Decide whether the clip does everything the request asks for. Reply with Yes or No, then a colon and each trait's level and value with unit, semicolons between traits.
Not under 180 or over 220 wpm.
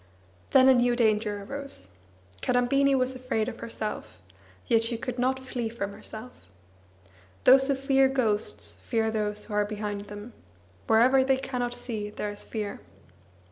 No: average, 150 wpm